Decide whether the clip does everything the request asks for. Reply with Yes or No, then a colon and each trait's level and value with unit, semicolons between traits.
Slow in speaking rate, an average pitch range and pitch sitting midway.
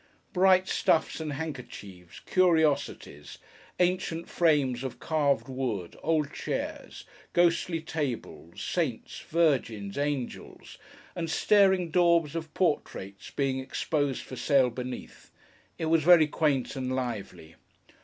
Yes: slow, 110 wpm; average, 4.6 semitones; medium, 145 Hz